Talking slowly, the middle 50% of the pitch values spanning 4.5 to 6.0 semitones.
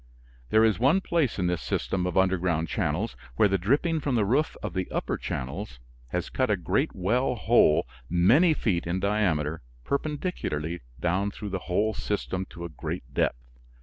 No: average, 175 wpm; average, 5.1 semitones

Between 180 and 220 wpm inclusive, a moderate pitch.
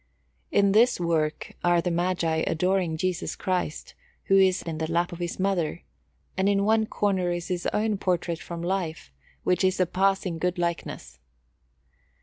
No: average, 160 wpm; medium, 180 Hz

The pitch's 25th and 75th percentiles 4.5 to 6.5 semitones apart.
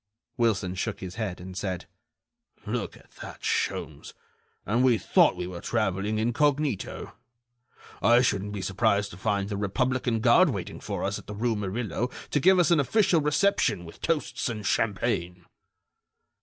Yes: average, 5.1 semitones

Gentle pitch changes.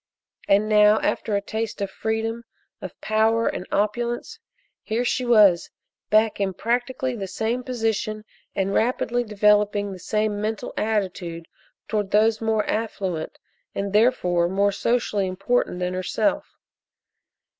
Yes: narrow, 2.2 semitones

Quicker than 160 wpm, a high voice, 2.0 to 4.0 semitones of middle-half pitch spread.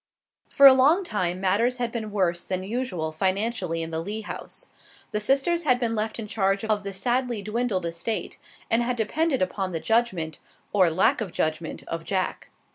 No: average, 185 wpm; high, 210 Hz; average, 4.6 semitones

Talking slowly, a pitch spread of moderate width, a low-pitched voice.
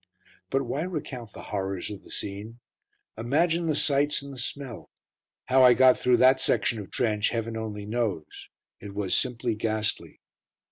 No: average, 160 wpm; average, 4.1 semitones; low, 120 Hz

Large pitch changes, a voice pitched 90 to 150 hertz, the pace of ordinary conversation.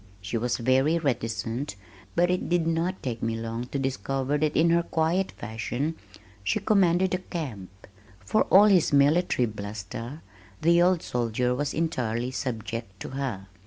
Yes: wide, 6.5 semitones; low, 135 Hz; average, 155 wpm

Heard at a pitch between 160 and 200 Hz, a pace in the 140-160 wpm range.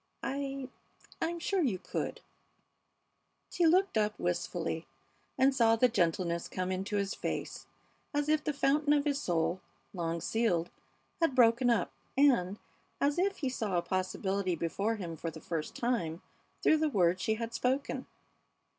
No: high, 225 Hz; average, 155 wpm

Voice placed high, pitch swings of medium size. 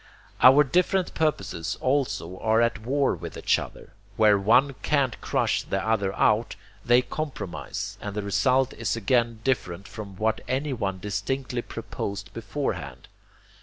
No: low, 115 Hz; average, 4.8 semitones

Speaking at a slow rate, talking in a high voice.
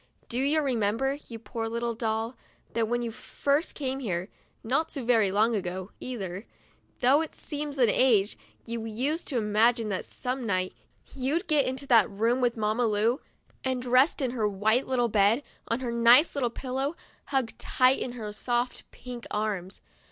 No: average, 175 wpm; high, 240 Hz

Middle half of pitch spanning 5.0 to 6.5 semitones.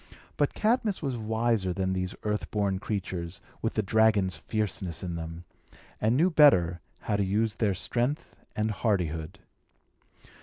No: average, 3.5 semitones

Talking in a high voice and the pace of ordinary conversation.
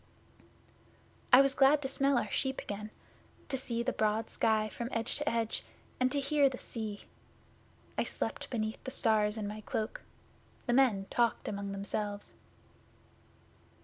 Yes: high, 230 Hz; average, 150 wpm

